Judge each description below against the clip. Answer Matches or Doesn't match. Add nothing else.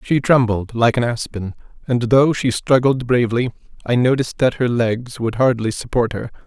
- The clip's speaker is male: Matches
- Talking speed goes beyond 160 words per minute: Matches